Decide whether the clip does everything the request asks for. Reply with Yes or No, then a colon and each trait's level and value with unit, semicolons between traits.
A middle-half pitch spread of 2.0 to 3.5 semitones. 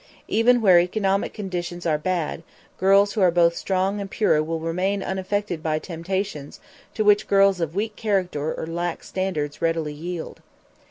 Yes: average, 3.2 semitones